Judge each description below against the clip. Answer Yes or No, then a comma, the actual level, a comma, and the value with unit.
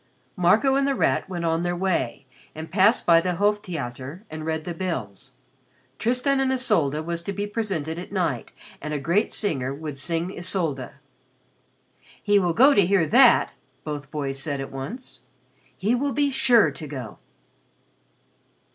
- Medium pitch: Yes, medium, 170 Hz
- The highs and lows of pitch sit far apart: Yes, wide, 5.8 semitones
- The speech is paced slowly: No, average, 165 wpm